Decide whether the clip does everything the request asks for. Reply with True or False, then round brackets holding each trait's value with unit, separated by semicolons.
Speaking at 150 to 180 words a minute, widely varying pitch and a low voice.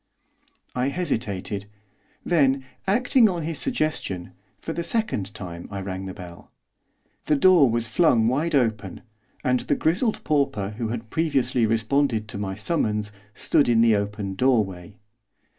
False (140 wpm; 7.0 semitones; 115 Hz)